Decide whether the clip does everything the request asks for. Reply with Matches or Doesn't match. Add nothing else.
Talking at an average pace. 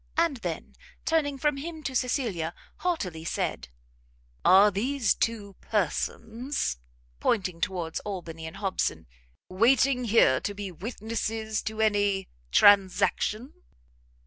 Doesn't match